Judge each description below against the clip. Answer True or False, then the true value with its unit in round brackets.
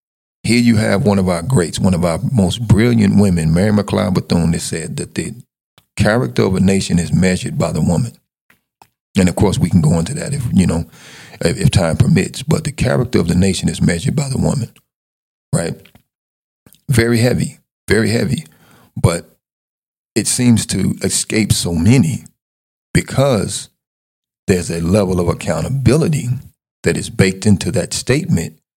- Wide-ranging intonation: False (4.3 semitones)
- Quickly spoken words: False (165 wpm)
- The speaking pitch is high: False (100 Hz)